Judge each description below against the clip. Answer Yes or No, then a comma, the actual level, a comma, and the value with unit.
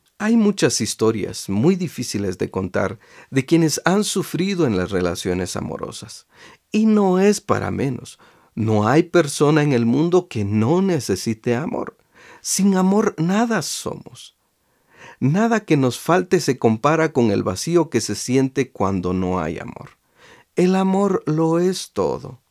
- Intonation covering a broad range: Yes, wide, 8.9 semitones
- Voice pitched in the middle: Yes, medium, 150 Hz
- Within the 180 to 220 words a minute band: No, average, 145 wpm